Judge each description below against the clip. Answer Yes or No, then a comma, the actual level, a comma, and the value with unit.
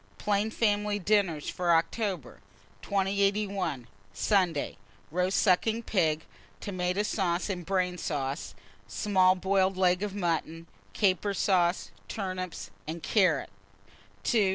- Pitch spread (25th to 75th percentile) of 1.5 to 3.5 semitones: Yes, average, 2.8 semitones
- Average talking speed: No, slow, 105 wpm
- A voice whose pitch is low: No, medium, 185 Hz